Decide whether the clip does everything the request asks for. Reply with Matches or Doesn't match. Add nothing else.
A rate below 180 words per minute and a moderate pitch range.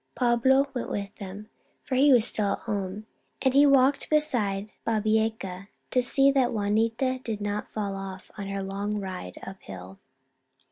Matches